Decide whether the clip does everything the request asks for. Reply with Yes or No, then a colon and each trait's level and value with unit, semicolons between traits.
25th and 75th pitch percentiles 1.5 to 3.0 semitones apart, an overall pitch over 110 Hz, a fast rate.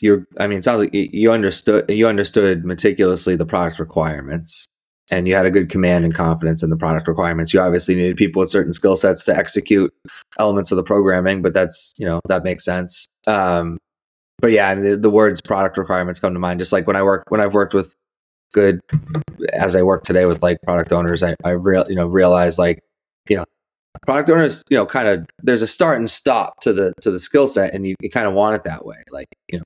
No: narrow, 2.5 semitones; very low, 95 Hz; fast, 235 wpm